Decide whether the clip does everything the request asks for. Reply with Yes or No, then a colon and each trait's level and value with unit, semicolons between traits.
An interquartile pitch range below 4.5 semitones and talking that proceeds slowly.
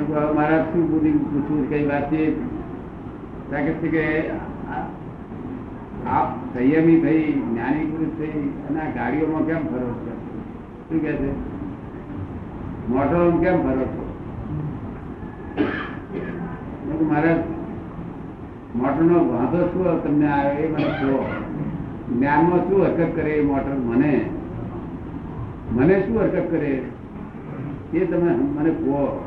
Yes: narrow, 2.5 semitones; slow, 55 wpm